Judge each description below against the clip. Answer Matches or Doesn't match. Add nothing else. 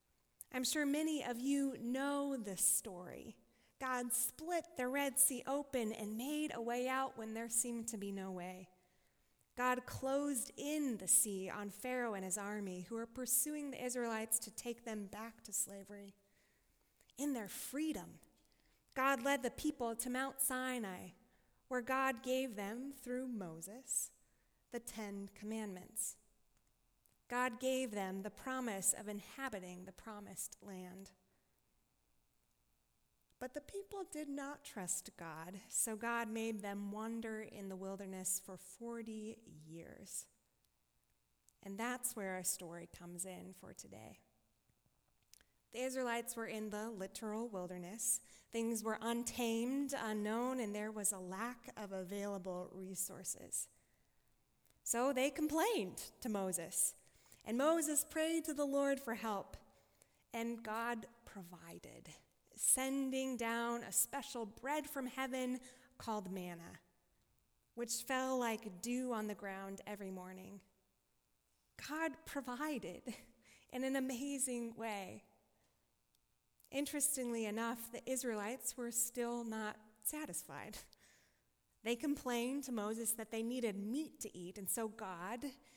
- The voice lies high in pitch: Matches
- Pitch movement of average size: Matches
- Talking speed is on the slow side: Matches